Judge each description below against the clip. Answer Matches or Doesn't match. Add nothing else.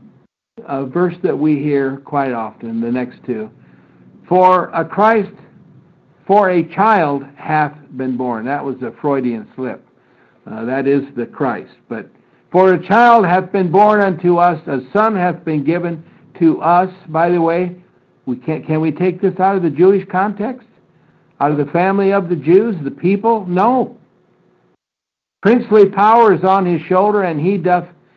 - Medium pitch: Matches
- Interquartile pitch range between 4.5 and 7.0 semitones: Matches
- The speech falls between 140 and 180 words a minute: Matches